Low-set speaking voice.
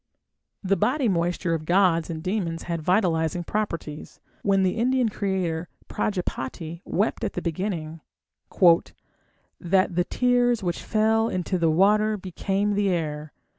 No: medium, 185 Hz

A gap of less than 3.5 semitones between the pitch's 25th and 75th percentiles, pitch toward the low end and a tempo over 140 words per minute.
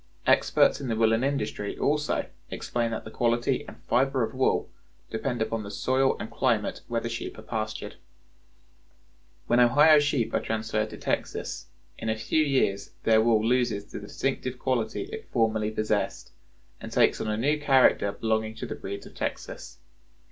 Yes: average, 3.1 semitones; low, 115 Hz; average, 170 wpm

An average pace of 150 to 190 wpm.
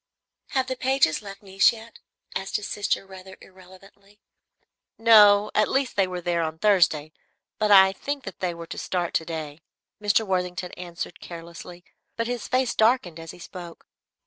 Yes: average, 170 wpm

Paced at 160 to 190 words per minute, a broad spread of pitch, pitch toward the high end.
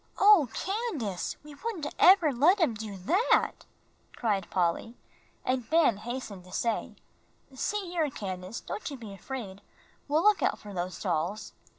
No: average, 150 wpm; wide, 9.0 semitones; high, 245 Hz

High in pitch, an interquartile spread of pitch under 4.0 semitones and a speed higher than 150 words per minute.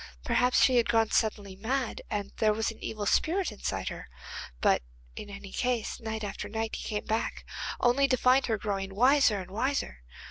Yes: high, 220 Hz; average, 3.4 semitones; average, 185 wpm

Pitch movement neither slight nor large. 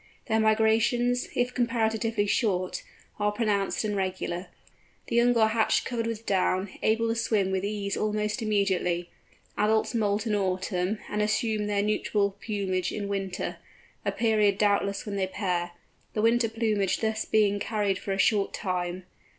No: narrow, 2.2 semitones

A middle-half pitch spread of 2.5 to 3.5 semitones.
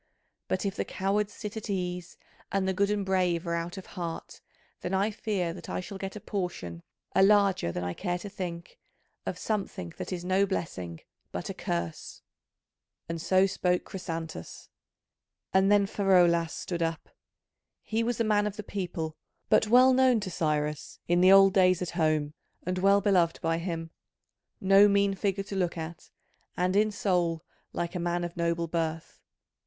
Yes: average, 2.9 semitones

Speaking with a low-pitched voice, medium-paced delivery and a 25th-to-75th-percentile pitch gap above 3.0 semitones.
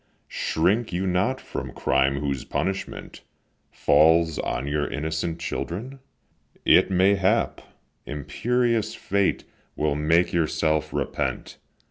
No: very low, 85 Hz; slow, 105 wpm; average, 4.6 semitones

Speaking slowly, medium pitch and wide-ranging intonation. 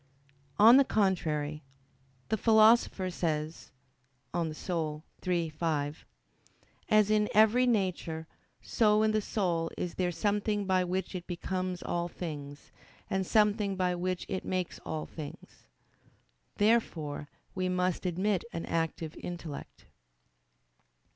No: slow, 120 wpm; medium, 180 Hz; average, 4.1 semitones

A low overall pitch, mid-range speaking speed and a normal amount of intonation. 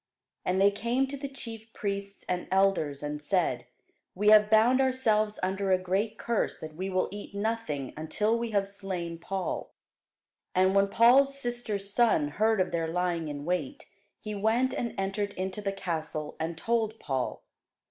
No: high, 200 Hz; average, 170 wpm; average, 3.7 semitones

